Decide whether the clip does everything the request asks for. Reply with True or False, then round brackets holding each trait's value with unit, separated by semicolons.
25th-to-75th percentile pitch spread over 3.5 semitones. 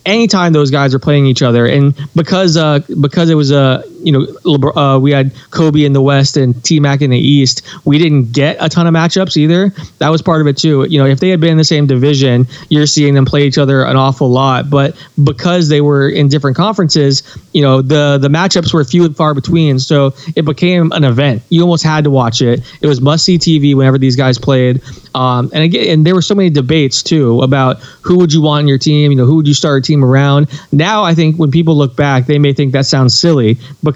False (2.8 semitones)